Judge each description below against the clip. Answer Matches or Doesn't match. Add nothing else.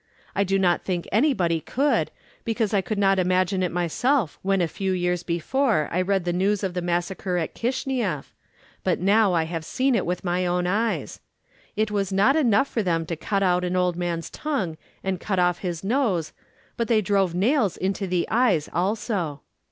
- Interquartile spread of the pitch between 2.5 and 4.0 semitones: Matches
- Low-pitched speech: Doesn't match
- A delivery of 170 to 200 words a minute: Matches